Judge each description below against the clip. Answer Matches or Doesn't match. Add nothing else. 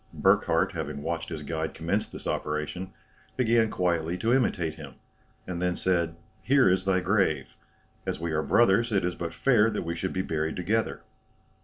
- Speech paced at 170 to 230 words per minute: Matches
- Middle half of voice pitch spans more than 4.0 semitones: Matches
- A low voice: Matches